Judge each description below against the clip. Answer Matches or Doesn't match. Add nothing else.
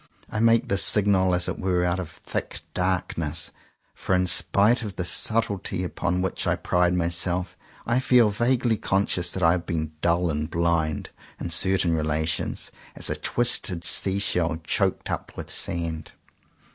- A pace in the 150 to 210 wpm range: Matches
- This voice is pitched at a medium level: Doesn't match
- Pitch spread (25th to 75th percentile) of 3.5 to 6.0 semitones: Doesn't match